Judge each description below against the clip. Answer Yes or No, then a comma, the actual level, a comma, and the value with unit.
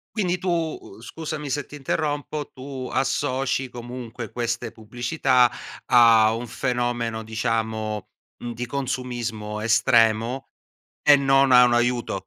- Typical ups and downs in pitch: Yes, average, 3.0 semitones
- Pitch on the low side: Yes, low, 120 Hz